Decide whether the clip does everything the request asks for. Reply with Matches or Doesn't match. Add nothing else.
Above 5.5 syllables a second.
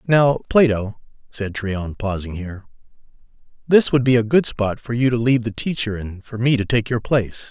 Doesn't match